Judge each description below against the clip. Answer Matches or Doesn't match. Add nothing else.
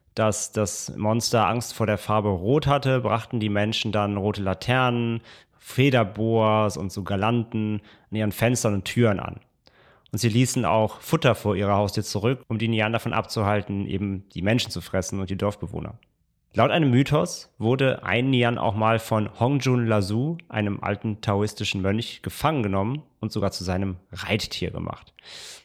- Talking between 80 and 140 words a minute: Doesn't match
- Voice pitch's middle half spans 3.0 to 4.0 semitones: Doesn't match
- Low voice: Matches